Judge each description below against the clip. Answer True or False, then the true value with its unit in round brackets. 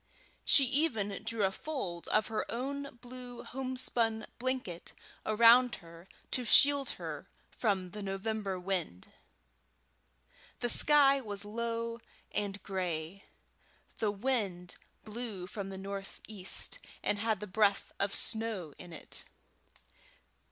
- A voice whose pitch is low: False (215 Hz)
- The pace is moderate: False (115 wpm)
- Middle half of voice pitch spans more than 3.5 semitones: True (3.9 semitones)